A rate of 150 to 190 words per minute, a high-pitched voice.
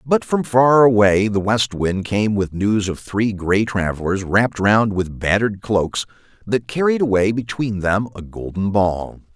No: average, 175 wpm; low, 105 Hz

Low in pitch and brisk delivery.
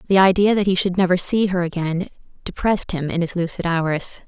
No: medium, 180 Hz; fast, 210 wpm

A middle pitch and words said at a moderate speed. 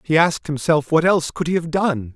No: medium, 155 Hz; fast, 250 wpm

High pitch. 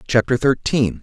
No: low, 115 Hz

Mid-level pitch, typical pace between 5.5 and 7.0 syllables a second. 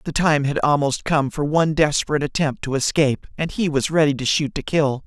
Yes: medium, 145 Hz; 5.8 syllables/s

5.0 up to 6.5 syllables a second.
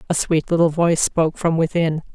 Yes: 6.0 syllables/s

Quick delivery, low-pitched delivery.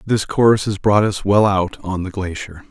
Yes: fast, 220 wpm; low, 100 Hz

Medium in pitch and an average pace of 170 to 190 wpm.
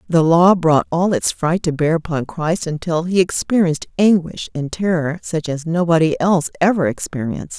Yes: medium, 165 Hz; average, 175 wpm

